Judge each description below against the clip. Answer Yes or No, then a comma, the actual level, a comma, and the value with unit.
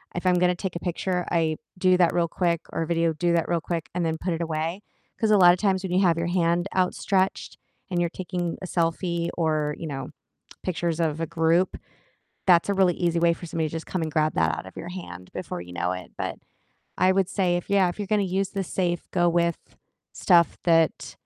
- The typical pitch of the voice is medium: Yes, medium, 170 Hz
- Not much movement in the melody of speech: Yes, narrow, 1.9 semitones